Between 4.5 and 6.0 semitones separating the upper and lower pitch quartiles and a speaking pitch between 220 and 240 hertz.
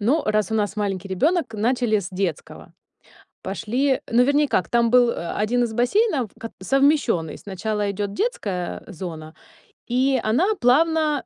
Yes: average, 5.3 semitones; high, 230 Hz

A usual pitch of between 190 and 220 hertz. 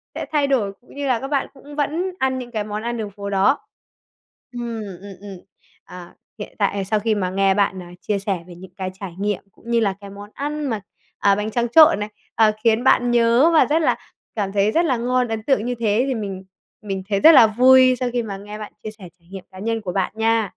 Yes: high, 215 Hz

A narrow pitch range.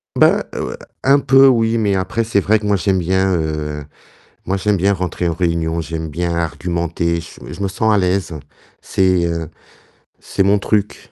No: average, 3.2 semitones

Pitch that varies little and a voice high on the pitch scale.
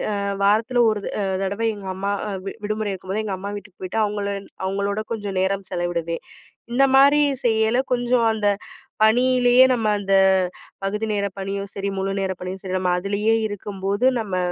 Yes: narrow, 2.3 semitones; high, 205 Hz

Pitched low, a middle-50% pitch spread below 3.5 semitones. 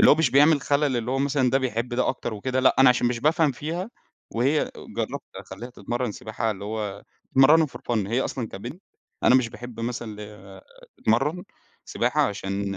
No: low, 125 Hz; average, 3.9 semitones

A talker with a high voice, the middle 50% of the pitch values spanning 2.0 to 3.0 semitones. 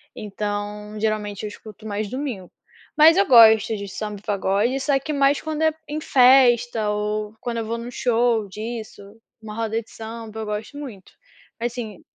Yes: high, 220 Hz; average, 2.7 semitones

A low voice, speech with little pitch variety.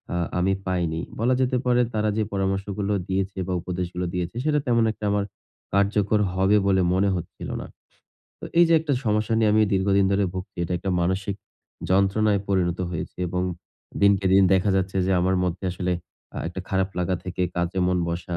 Yes: very low, 95 Hz; narrow, 2.1 semitones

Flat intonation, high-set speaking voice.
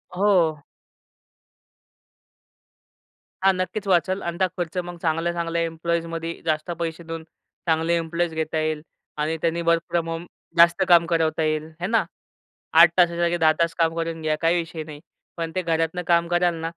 No: narrow, 1.1 semitones; medium, 165 Hz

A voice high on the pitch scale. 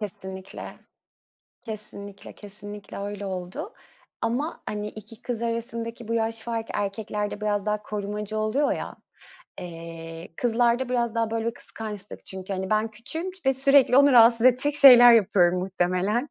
Yes: high, 215 Hz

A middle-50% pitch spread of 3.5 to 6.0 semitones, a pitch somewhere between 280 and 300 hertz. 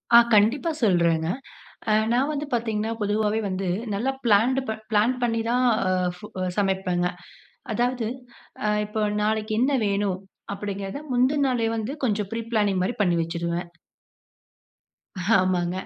No: average, 3.8 semitones; high, 210 Hz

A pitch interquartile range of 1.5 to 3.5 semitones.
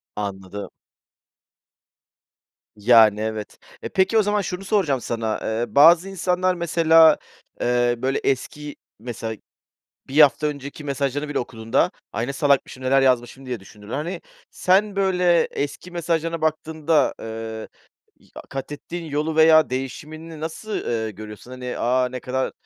No: average, 5.3 semitones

